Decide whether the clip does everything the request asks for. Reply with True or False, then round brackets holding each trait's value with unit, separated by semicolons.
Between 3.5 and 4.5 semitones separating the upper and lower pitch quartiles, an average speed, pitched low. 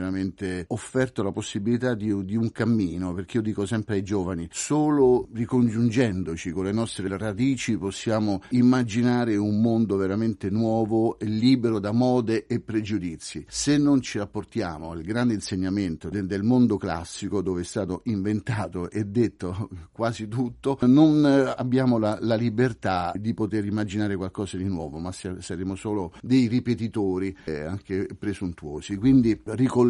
True (3.8 semitones; 140 wpm; 105 Hz)